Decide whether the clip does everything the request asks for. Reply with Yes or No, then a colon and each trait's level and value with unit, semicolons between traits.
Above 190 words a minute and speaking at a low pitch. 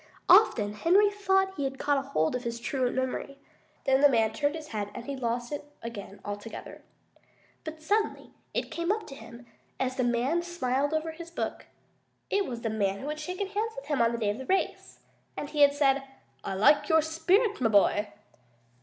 No: average, 200 wpm; very high, 275 Hz